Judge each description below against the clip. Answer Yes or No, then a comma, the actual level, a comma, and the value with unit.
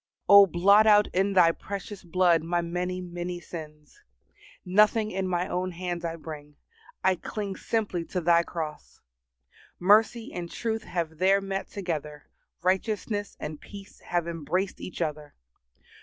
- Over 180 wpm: No, average, 140 wpm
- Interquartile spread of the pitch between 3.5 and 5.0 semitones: No, average, 2.9 semitones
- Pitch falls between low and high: Yes, medium, 180 Hz